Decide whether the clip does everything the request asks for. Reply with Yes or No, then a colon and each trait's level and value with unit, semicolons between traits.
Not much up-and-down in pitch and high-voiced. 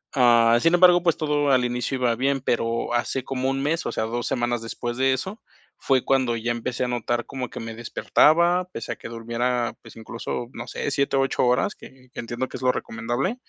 No: narrow, 2.3 semitones; low, 125 Hz